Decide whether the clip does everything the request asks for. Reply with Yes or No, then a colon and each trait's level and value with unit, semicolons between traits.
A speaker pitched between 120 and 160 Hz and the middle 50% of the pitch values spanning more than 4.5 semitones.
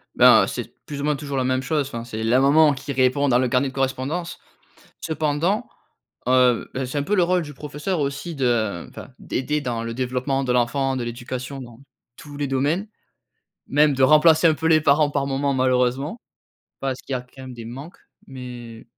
No: low, 135 Hz; average, 2.8 semitones